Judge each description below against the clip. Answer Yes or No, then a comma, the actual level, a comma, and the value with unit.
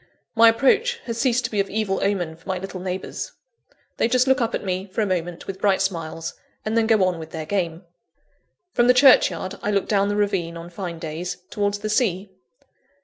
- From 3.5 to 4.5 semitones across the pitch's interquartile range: Yes, average, 3.9 semitones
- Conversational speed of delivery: No, fast, 210 wpm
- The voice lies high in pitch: Yes, high, 195 Hz